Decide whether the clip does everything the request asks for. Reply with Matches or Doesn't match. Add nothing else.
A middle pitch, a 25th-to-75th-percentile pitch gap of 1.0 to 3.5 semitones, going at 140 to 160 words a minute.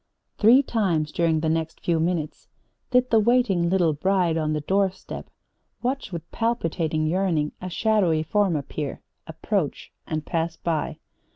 Doesn't match